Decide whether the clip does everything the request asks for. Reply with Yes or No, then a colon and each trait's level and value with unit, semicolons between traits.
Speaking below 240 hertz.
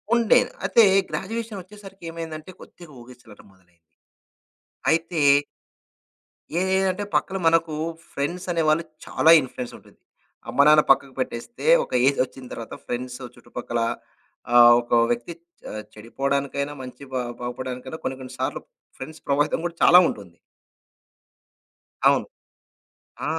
Yes: medium, 140 Hz